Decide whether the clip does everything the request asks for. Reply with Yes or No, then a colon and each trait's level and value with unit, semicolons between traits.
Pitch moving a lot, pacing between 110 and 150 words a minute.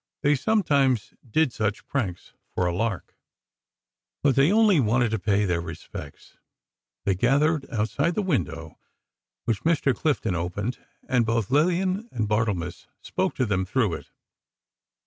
Yes: wide, 6.5 semitones; average, 140 wpm